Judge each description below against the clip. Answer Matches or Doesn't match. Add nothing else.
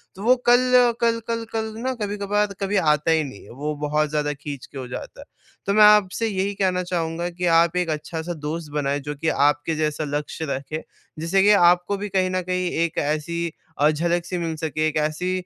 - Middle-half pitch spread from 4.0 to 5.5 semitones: Matches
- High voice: Doesn't match